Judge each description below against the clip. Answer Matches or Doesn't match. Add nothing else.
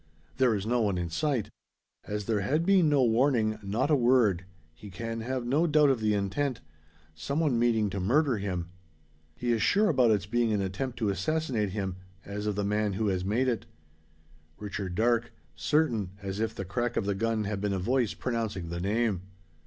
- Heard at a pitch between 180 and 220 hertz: Doesn't match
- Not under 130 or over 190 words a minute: Doesn't match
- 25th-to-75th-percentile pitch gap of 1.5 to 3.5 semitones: Doesn't match